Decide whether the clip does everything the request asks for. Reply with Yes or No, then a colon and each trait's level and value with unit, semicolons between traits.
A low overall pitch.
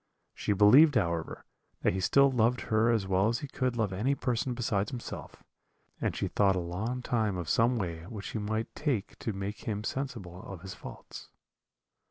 Yes: low, 110 Hz